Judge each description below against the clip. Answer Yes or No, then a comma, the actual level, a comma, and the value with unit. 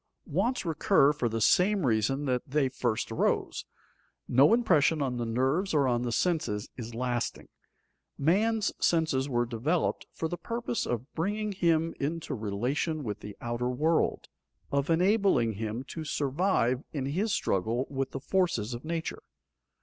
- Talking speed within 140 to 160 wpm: Yes, average, 150 wpm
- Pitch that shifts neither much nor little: No, wide, 5.8 semitones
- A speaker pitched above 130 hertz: Yes, medium, 140 Hz